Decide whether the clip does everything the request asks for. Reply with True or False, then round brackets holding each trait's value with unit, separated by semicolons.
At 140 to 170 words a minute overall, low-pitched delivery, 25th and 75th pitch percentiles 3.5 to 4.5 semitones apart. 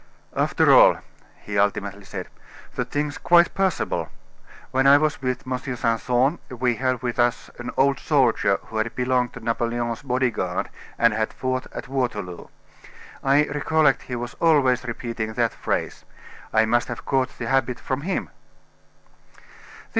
False (150 wpm; 125 Hz; 2.8 semitones)